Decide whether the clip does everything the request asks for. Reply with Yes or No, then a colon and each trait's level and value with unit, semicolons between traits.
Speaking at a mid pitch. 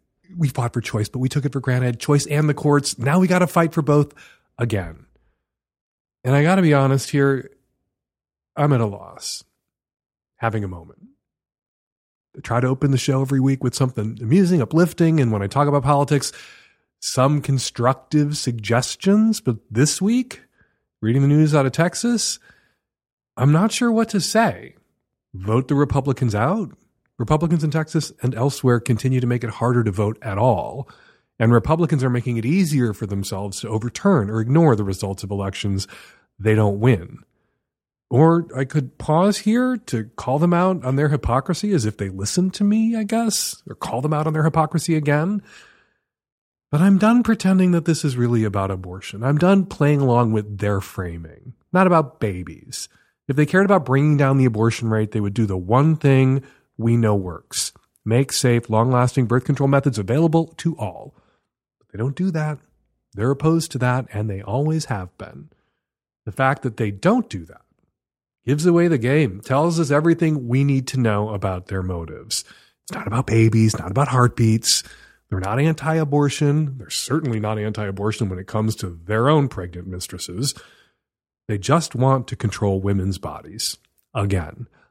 No: low, 130 Hz